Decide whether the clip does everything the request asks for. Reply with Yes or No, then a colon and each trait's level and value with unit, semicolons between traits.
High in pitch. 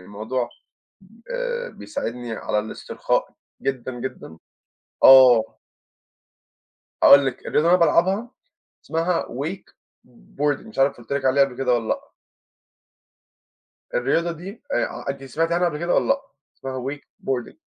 No: medium, 140 Hz